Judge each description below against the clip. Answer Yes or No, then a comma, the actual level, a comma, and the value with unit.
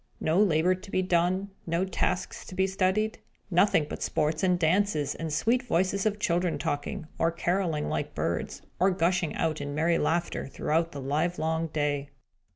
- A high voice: No, medium, 170 Hz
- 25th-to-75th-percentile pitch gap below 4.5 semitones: Yes, average, 3.1 semitones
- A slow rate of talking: No, average, 165 wpm